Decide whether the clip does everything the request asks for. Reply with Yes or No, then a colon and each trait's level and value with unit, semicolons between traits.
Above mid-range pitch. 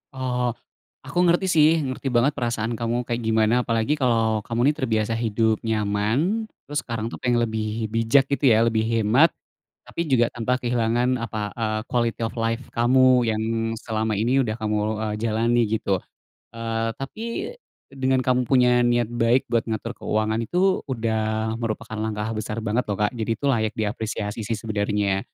No: low, 115 Hz